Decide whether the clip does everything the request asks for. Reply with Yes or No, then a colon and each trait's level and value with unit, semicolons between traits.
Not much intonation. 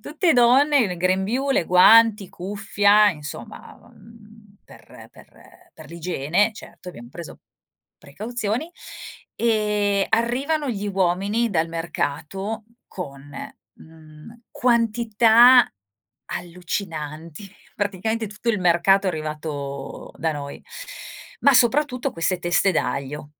No: wide, 5.5 semitones